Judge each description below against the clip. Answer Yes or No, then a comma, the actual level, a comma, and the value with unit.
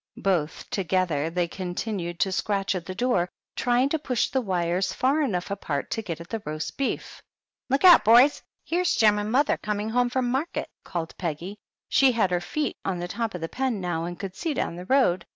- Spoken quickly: Yes, fast, 210 wpm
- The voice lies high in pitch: Yes, high, 195 Hz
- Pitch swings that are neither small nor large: No, wide, 6.0 semitones